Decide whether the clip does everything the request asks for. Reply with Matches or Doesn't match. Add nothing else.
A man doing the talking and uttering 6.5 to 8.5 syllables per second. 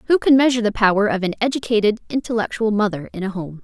Doesn't match